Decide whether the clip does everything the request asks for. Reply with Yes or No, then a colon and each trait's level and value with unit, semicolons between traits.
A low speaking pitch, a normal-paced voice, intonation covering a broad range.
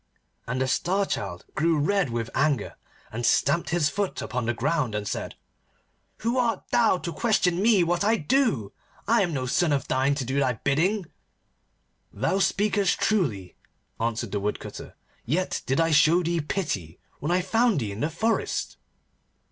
No: medium, 155 Hz; average, 170 wpm; wide, 7.3 semitones